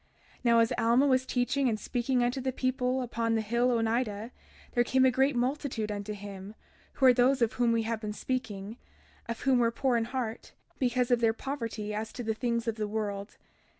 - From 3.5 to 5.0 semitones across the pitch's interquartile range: No, narrow, 2.5 semitones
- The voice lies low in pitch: No, high, 235 Hz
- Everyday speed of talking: No, fast, 210 wpm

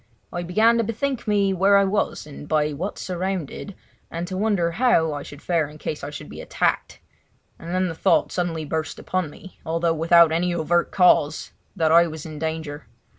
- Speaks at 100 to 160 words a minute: No, average, 195 wpm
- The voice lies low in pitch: No, medium, 170 Hz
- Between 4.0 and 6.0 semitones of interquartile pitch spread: No, average, 3.2 semitones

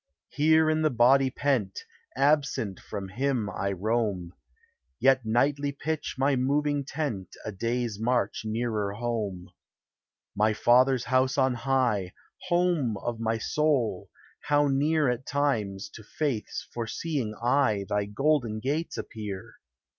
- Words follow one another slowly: Yes, slow, 125 wpm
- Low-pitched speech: Yes, low, 125 Hz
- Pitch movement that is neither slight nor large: Yes, average, 4.8 semitones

